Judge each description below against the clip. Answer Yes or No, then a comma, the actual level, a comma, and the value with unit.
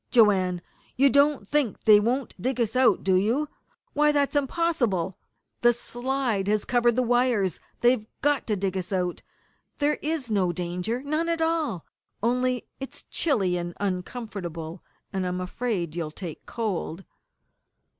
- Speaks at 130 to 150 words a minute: Yes, average, 145 wpm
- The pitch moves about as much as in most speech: No, wide, 6.3 semitones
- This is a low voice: No, high, 230 Hz